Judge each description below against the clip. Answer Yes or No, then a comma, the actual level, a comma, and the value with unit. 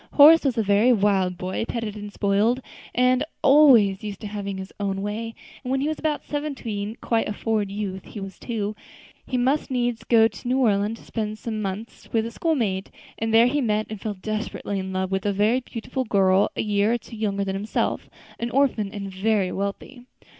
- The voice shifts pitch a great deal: No, average, 3.3 semitones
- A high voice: Yes, high, 215 Hz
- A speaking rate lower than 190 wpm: No, fast, 205 wpm